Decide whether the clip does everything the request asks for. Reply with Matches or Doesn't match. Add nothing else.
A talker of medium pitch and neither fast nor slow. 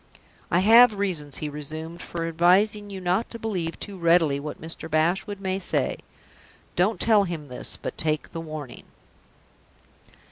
Matches